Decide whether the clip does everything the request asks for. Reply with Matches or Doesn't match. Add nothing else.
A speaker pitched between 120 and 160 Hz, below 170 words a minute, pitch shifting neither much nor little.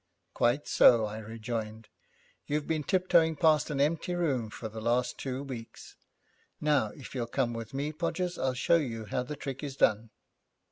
Doesn't match